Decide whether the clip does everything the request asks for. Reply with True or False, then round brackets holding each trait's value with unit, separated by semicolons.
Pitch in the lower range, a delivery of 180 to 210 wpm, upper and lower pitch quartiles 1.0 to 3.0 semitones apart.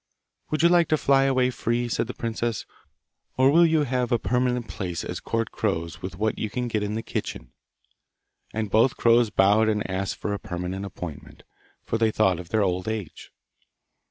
False (110 Hz; 190 wpm; 4.2 semitones)